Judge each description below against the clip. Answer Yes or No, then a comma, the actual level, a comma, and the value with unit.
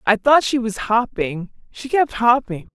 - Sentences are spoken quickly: No, average, 175 wpm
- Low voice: No, high, 235 Hz